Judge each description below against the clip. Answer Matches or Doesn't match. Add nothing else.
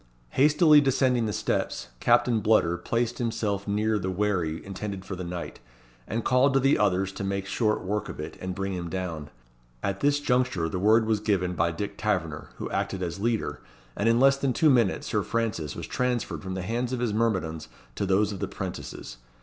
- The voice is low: Matches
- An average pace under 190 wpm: Doesn't match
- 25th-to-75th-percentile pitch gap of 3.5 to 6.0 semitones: Matches